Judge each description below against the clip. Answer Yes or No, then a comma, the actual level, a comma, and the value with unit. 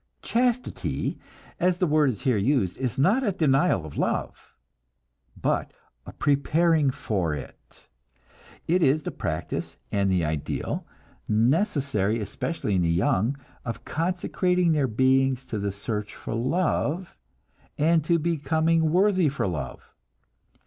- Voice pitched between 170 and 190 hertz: No, medium, 140 Hz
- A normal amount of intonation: No, wide, 8.1 semitones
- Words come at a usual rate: No, slow, 130 wpm